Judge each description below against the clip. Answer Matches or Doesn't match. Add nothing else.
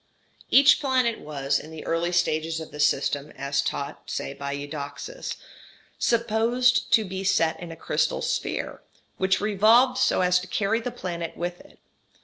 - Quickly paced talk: Doesn't match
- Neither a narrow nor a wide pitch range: Doesn't match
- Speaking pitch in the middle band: Matches